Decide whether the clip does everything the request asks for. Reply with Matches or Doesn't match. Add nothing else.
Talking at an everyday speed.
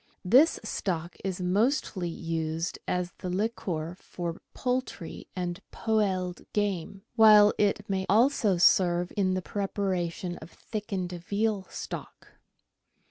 Doesn't match